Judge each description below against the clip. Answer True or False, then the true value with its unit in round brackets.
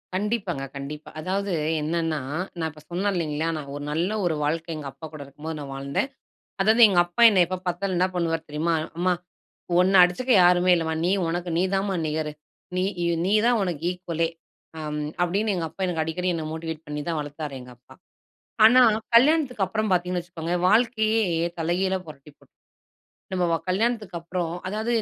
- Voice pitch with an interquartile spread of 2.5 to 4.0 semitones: True (3.3 semitones)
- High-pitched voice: False (175 Hz)